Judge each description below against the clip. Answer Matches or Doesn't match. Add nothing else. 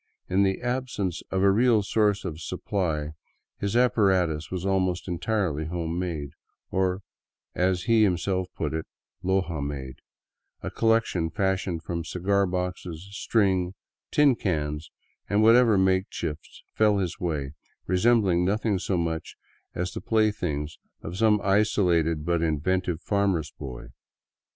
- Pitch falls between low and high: Doesn't match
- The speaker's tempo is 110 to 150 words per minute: Matches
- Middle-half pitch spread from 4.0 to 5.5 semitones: Doesn't match